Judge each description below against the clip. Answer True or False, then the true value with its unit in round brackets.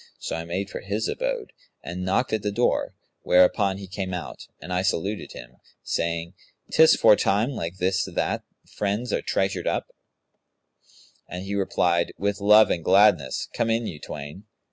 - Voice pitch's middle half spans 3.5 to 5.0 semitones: False (2.8 semitones)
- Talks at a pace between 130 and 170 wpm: True (165 wpm)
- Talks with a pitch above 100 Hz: False (95 Hz)